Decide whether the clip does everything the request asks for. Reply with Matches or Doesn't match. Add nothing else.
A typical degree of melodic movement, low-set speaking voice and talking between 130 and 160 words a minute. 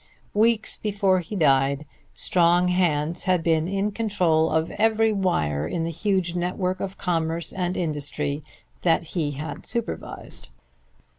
Doesn't match